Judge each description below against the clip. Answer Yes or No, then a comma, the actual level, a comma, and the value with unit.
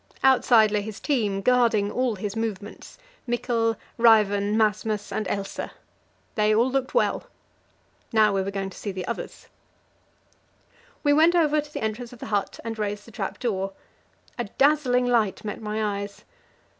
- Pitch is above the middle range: Yes, high, 220 Hz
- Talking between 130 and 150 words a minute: No, average, 160 wpm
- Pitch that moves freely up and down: No, average, 3.2 semitones